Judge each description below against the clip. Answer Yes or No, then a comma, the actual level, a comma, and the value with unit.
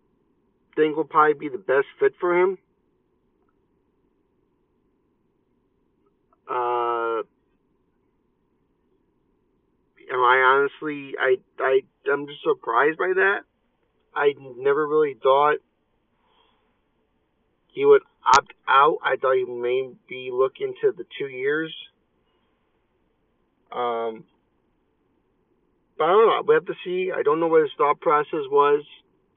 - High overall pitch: Yes, very high, 365 Hz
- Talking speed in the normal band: No, slow, 110 wpm